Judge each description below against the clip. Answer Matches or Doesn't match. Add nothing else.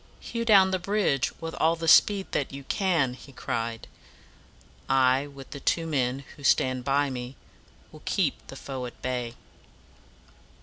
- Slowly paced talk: Doesn't match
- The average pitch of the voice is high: Doesn't match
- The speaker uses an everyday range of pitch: Matches